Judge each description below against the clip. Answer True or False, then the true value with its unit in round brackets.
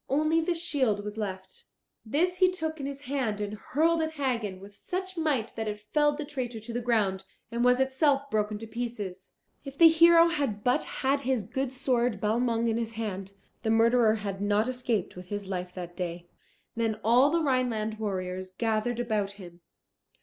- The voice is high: True (230 Hz)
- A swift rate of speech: False (185 wpm)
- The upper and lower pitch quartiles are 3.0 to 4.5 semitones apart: False (5.1 semitones)